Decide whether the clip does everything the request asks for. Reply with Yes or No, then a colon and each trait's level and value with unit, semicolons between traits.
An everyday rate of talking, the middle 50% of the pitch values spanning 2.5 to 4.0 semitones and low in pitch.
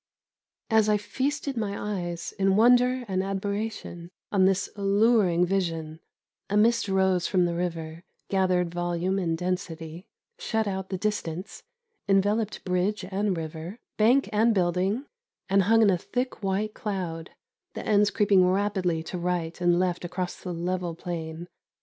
No: average, 145 wpm; average, 3.0 semitones; high, 190 Hz